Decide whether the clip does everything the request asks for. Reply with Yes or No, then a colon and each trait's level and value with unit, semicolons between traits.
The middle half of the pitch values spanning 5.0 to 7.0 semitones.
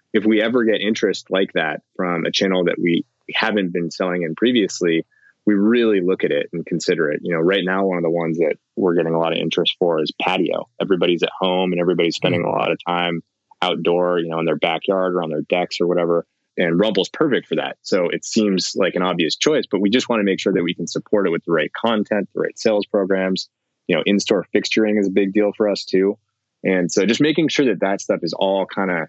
No: average, 3.2 semitones